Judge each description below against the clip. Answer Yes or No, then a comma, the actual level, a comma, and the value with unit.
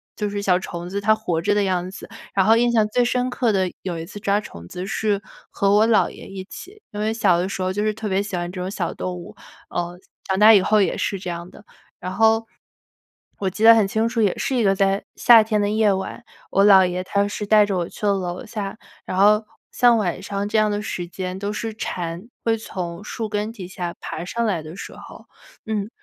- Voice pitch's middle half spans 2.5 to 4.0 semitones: Yes, average, 2.8 semitones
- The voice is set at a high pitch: Yes, high, 200 Hz